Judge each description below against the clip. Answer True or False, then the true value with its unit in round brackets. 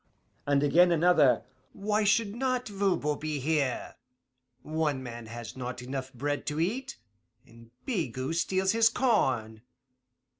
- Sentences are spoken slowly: True (125 wpm)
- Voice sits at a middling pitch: True (150 Hz)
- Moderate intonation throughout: False (7.5 semitones)